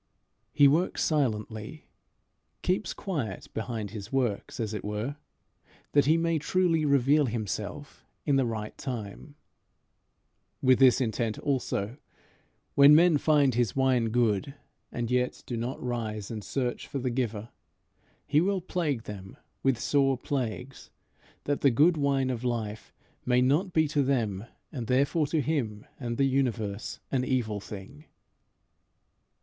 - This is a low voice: Yes, low, 125 Hz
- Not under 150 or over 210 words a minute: No, average, 140 wpm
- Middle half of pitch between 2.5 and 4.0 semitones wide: No, average, 4.4 semitones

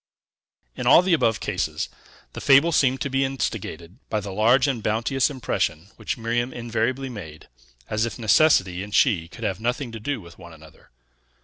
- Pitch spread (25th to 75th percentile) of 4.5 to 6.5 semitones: Yes, average, 5.3 semitones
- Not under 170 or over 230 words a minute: Yes, average, 180 wpm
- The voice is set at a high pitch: No, low, 115 Hz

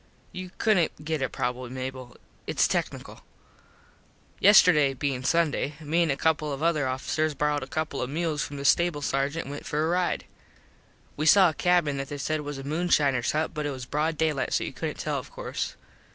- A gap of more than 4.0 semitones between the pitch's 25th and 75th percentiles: No, average, 2.8 semitones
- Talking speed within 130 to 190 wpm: No, average, 200 wpm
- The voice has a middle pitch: Yes, medium, 150 Hz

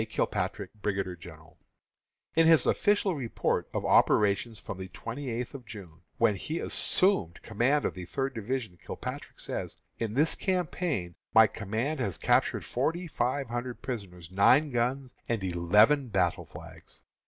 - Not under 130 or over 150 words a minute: Yes, average, 145 wpm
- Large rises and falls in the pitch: Yes, wide, 6.2 semitones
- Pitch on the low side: Yes, low, 115 Hz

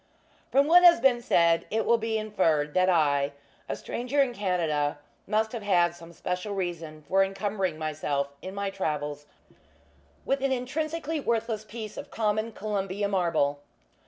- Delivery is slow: No, average, 155 wpm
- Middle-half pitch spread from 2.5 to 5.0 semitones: No, wide, 5.5 semitones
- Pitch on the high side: Yes, high, 195 Hz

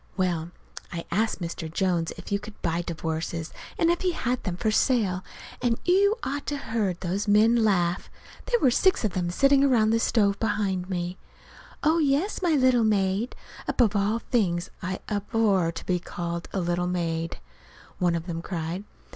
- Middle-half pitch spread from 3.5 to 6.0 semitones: Yes, average, 5.2 semitones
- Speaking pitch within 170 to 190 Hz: No, high, 200 Hz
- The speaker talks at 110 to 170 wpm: No, average, 180 wpm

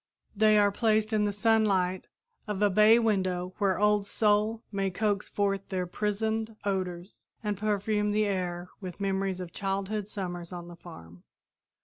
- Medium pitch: No, high, 200 Hz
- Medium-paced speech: Yes, average, 155 wpm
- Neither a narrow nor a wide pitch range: No, narrow, 2.3 semitones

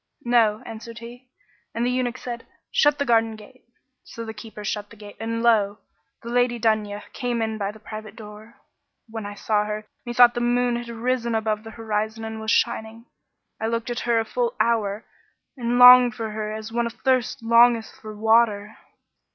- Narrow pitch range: Yes, narrow, 1.8 semitones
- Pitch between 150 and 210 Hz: No, high, 225 Hz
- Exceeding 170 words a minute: Yes, average, 185 wpm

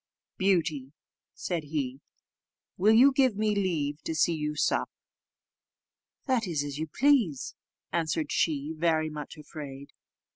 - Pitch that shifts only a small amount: No, average, 4.8 semitones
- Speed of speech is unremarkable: No, slow, 125 wpm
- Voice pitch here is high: No, medium, 160 Hz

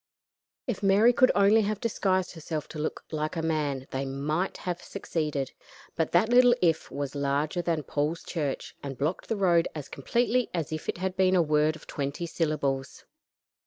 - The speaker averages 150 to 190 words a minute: Yes, average, 180 wpm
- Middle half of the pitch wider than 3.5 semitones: Yes, average, 4.3 semitones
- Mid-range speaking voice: Yes, medium, 160 Hz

